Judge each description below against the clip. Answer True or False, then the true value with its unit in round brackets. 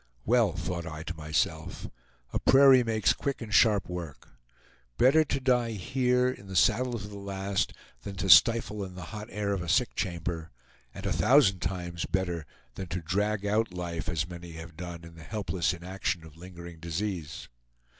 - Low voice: True (95 Hz)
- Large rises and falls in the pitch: False (4.1 semitones)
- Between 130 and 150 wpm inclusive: False (180 wpm)